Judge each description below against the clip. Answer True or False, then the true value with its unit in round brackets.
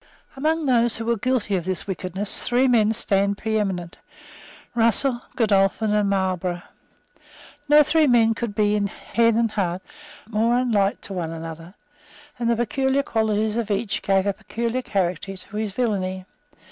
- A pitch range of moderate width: True (3.4 semitones)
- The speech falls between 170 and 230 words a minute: False (155 wpm)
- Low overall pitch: False (215 Hz)